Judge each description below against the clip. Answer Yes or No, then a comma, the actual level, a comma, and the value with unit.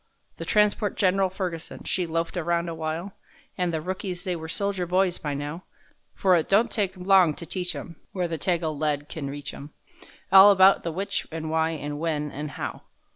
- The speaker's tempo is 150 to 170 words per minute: No, average, 185 wpm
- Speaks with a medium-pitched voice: Yes, medium, 170 Hz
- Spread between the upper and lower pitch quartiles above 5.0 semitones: No, average, 3.1 semitones